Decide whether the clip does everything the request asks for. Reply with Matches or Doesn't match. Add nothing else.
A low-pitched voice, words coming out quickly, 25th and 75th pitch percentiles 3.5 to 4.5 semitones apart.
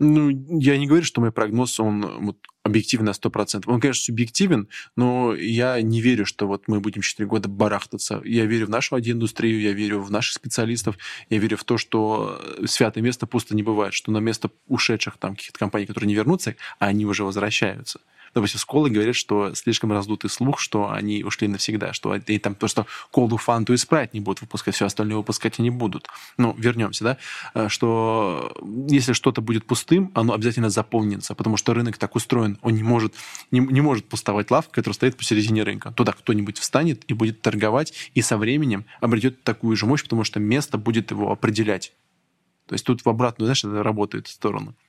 Doesn't match